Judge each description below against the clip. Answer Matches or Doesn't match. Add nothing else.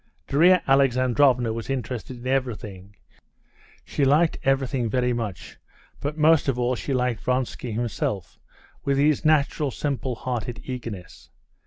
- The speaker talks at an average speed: Doesn't match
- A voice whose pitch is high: Doesn't match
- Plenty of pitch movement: Doesn't match